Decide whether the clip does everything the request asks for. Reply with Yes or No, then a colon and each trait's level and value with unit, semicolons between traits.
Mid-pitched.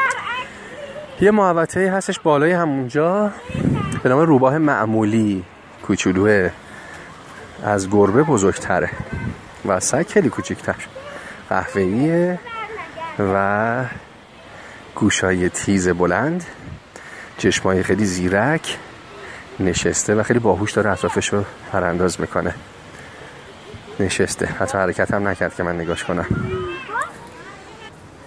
No: low, 110 Hz